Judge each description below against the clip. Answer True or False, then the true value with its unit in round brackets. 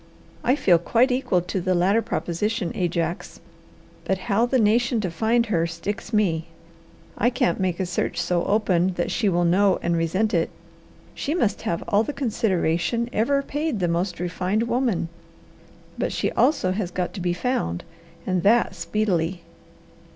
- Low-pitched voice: False (190 Hz)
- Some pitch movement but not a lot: True (4.7 semitones)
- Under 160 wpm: False (165 wpm)